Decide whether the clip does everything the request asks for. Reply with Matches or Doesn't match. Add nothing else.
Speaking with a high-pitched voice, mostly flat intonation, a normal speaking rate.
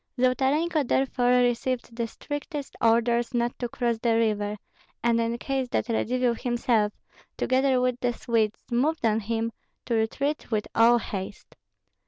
Matches